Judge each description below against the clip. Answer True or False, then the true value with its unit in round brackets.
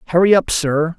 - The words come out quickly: False (185 wpm)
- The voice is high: False (170 Hz)